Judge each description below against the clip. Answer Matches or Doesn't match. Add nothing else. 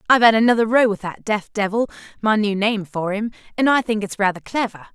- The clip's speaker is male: Doesn't match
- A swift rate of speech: Matches